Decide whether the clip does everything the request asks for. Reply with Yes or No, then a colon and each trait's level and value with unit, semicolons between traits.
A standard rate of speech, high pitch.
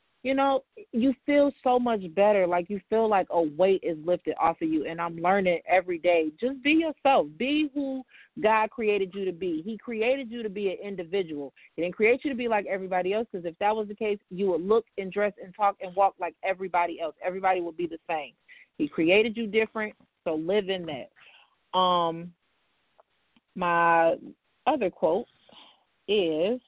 Yes: average, 190 wpm; high, 200 Hz